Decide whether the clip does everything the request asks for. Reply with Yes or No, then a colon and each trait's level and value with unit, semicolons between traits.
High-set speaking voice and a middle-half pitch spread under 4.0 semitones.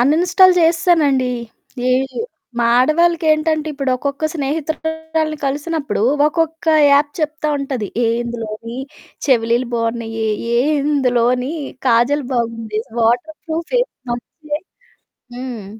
No: very high, 280 Hz; average, 4.7 semitones